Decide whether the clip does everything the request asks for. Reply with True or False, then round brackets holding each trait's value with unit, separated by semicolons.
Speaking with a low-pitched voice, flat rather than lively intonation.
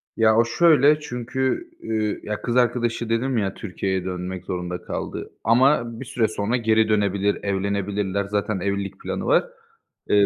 False (110 Hz; 3.1 semitones)